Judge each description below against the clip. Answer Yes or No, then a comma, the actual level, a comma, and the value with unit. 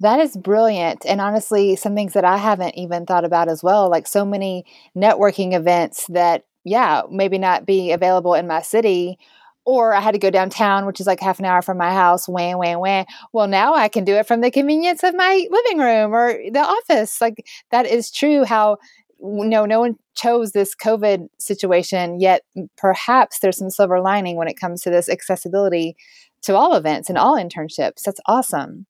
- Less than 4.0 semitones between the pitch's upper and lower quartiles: Yes, average, 3.5 semitones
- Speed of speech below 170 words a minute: No, average, 200 wpm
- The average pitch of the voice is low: No, high, 195 Hz